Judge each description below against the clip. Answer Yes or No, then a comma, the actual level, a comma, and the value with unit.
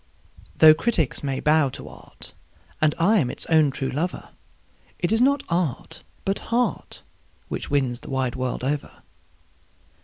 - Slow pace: No, average, 150 wpm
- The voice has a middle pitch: Yes, medium, 155 Hz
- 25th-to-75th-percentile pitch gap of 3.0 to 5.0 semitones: No, wide, 5.5 semitones